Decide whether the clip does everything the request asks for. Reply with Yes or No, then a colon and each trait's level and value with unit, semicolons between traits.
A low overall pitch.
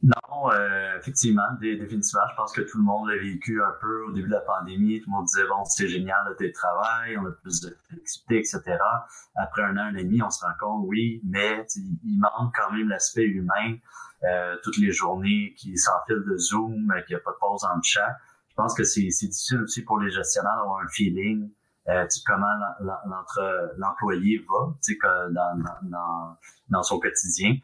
Yes: low, 105 Hz